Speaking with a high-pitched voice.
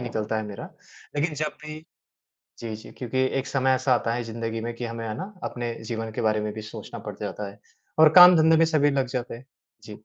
No: low, 120 Hz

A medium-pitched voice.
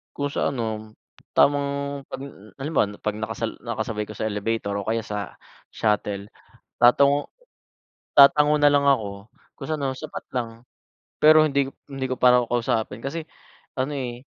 No: low, 125 Hz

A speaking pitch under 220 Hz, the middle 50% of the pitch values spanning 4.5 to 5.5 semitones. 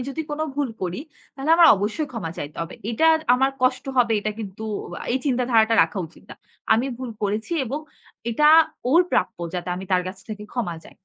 No: high, 230 Hz; average, 5.1 semitones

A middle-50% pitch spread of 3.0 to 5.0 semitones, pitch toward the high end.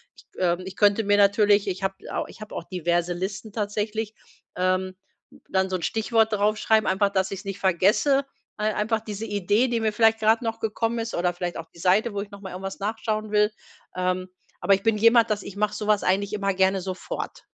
No: narrow, 2.4 semitones; high, 205 Hz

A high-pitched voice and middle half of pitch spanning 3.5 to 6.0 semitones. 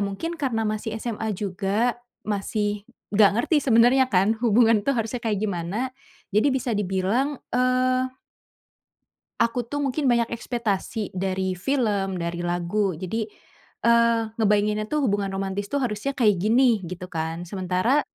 Yes: high, 215 Hz; average, 3.9 semitones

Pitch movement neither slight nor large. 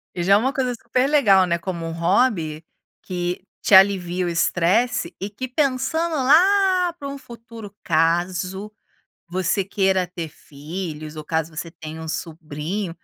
No: wide, 6.6 semitones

